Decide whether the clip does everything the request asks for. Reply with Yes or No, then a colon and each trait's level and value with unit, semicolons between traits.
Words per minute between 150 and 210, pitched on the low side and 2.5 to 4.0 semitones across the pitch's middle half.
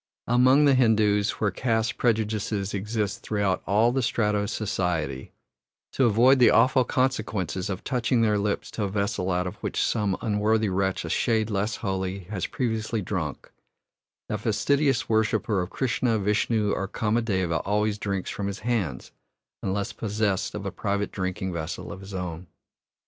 Yes: average, 160 wpm; low, 105 Hz; average, 2.9 semitones